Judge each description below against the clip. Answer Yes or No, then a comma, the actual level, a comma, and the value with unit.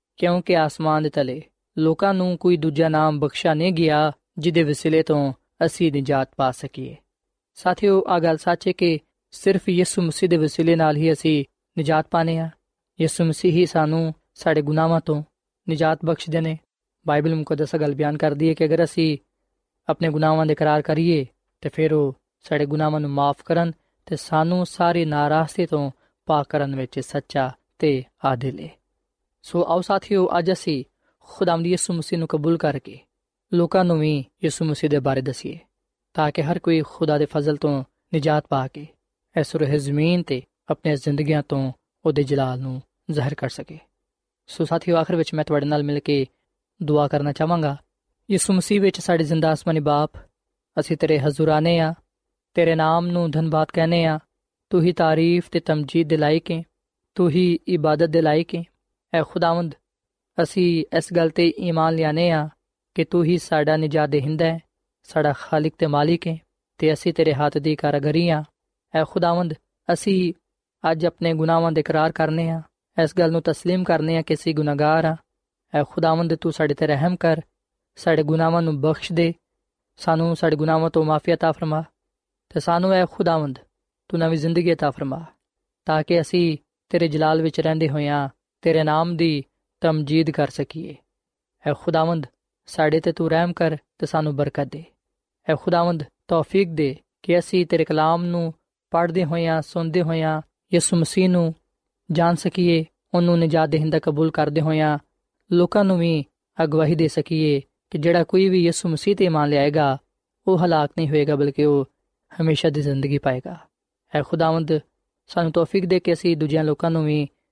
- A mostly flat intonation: Yes, narrow, 2.0 semitones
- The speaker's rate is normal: No, fast, 170 wpm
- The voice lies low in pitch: No, medium, 160 Hz